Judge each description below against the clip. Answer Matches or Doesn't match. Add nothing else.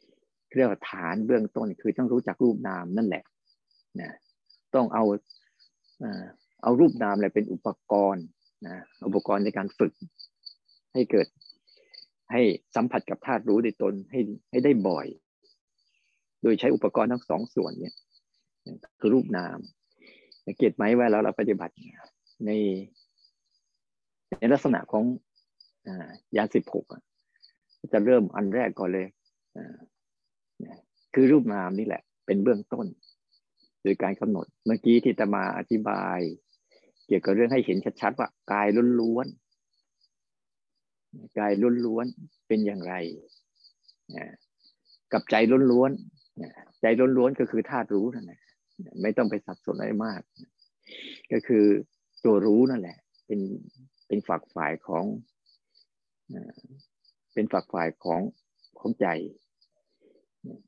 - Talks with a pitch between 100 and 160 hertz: Matches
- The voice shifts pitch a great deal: Doesn't match